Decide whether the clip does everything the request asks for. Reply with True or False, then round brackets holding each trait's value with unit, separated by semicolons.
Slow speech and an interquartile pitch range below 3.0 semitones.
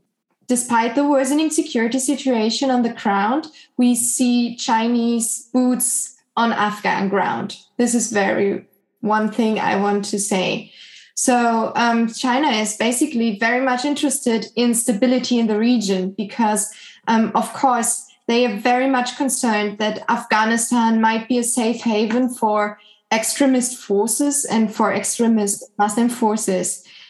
False (135 wpm; 2.6 semitones)